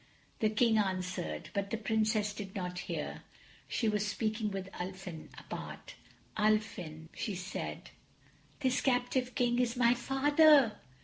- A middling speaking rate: No, slow, 130 wpm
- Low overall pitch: No, high, 215 Hz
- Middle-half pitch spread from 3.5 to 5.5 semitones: Yes, average, 4.2 semitones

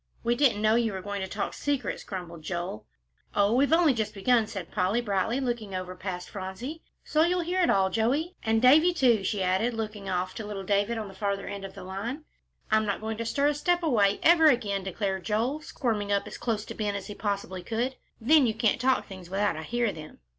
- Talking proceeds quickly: Yes, fast, 225 wpm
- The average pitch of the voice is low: No, high, 215 Hz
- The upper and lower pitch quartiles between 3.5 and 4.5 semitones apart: Yes, average, 4.2 semitones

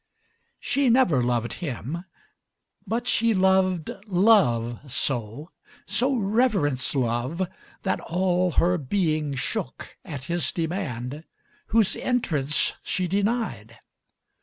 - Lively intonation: Yes, wide, 6.9 semitones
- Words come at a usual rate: No, slow, 90 wpm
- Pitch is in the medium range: Yes, medium, 175 Hz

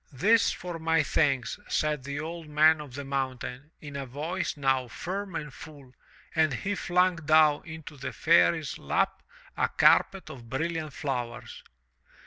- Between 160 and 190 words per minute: No, average, 150 wpm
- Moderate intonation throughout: Yes, average, 3.3 semitones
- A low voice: No, medium, 150 Hz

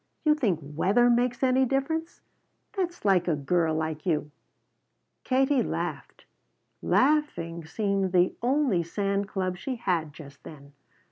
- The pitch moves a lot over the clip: Yes, wide, 7.8 semitones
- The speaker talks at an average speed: No, slow, 130 wpm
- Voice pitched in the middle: No, high, 195 Hz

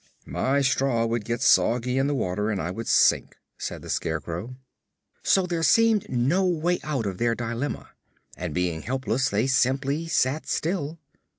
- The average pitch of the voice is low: Yes, low, 130 Hz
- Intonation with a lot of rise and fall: No, average, 4.8 semitones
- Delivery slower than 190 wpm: Yes, average, 165 wpm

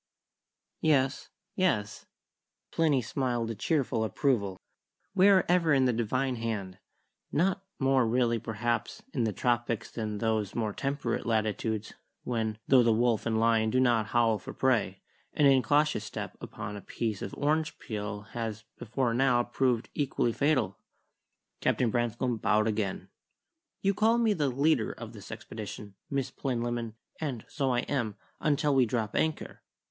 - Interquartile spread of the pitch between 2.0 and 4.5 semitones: Yes, average, 3.7 semitones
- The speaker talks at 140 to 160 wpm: Yes, average, 150 wpm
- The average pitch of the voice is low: Yes, low, 120 Hz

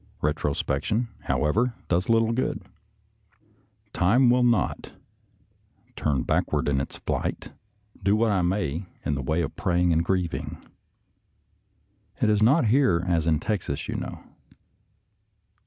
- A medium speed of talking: No, slow, 130 wpm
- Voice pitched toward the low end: Yes, very low, 90 Hz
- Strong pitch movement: Yes, wide, 6.3 semitones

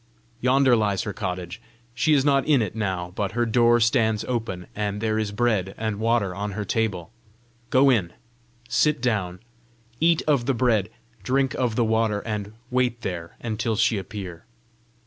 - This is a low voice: Yes, low, 110 Hz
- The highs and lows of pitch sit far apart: No, average, 3.1 semitones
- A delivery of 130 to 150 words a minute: No, average, 165 wpm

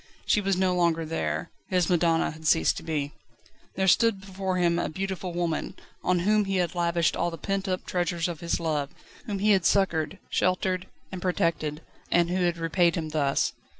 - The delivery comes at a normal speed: Yes, average, 190 wpm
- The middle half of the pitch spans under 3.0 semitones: Yes, narrow, 2.4 semitones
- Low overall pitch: No, medium, 175 Hz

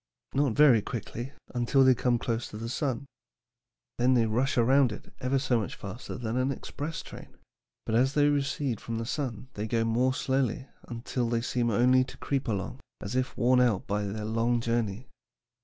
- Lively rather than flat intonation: No, narrow, 2.5 semitones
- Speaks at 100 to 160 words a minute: No, average, 190 wpm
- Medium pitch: No, low, 120 Hz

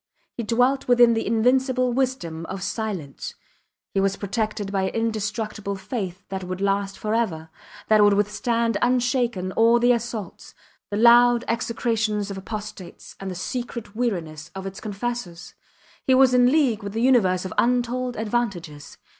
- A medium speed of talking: Yes, average, 150 wpm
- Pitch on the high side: Yes, high, 220 Hz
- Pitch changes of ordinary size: Yes, average, 3.8 semitones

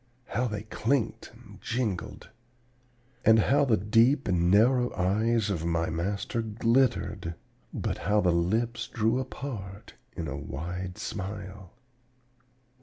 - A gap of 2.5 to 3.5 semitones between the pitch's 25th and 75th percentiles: No, average, 4.3 semitones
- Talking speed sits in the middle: No, slow, 120 wpm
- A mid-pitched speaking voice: No, low, 105 Hz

